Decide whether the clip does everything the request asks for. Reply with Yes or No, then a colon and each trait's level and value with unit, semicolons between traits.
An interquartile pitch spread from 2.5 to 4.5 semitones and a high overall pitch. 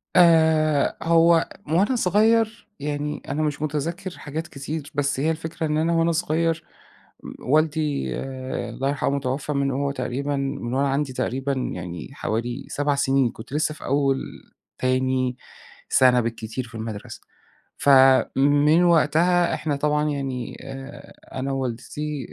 No: average, 3.0 semitones; medium, 145 Hz